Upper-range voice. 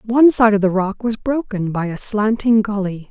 Yes: high, 215 Hz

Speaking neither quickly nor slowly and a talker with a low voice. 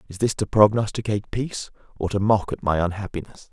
Yes: average, 190 wpm; low, 100 Hz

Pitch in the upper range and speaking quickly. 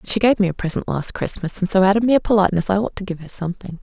Yes: high, 195 Hz; fast, 315 wpm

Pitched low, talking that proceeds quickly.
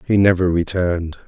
No: very low, 90 Hz; average, 140 wpm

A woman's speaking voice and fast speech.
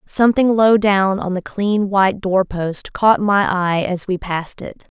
No: female; average, 190 wpm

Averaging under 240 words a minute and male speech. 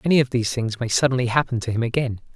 No: fast, 255 wpm; male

